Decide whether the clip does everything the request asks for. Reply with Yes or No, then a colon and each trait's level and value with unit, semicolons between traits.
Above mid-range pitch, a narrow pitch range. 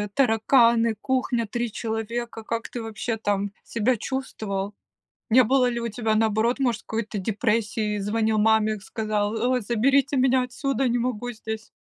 Yes: high, 225 Hz; narrow, 2.3 semitones